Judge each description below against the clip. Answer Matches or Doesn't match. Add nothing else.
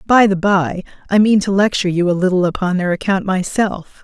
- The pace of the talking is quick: Matches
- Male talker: Doesn't match